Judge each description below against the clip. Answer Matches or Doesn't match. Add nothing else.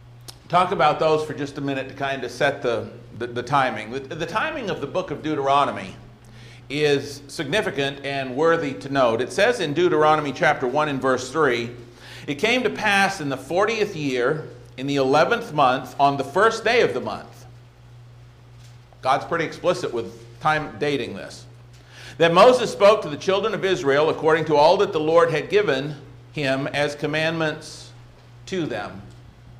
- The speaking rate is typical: Matches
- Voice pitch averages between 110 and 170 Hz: Matches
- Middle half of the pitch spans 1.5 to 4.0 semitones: Doesn't match